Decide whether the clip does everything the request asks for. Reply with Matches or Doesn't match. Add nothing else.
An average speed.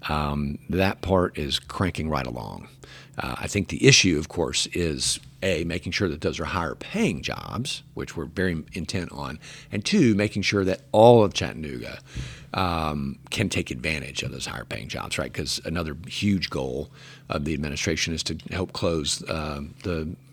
Matches